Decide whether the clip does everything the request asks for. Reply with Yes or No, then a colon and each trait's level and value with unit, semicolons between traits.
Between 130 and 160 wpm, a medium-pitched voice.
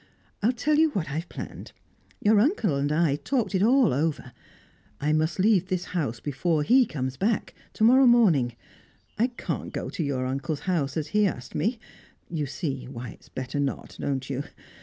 No: average, 185 wpm; medium, 160 Hz